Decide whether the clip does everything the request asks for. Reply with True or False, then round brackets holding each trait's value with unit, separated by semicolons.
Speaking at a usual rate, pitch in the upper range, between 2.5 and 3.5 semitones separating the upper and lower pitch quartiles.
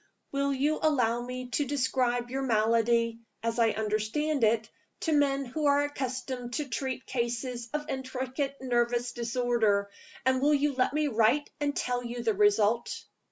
True (160 wpm; 250 Hz; 3.1 semitones)